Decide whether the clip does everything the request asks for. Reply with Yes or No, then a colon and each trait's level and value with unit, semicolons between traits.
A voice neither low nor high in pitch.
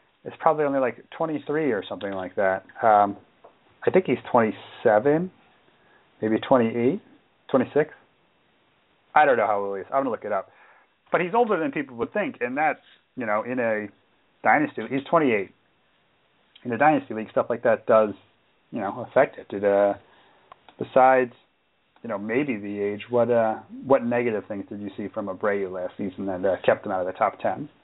No: low, 110 Hz